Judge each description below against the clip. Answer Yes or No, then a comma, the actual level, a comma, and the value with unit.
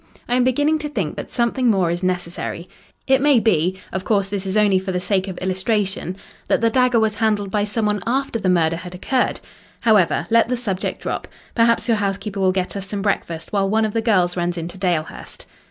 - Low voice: No, high, 200 Hz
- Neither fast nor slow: No, fast, 220 wpm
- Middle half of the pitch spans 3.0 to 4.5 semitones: Yes, average, 3.8 semitones